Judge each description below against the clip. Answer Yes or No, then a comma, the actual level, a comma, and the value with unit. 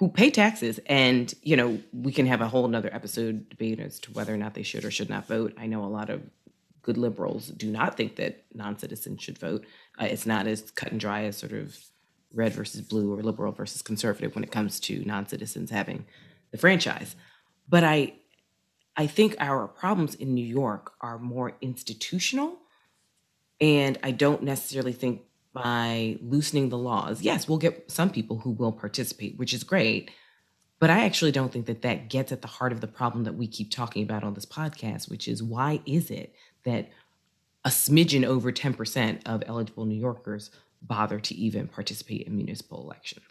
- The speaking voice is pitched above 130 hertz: No, low, 120 Hz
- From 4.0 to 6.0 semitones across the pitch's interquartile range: Yes, average, 4.6 semitones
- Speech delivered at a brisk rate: No, average, 195 wpm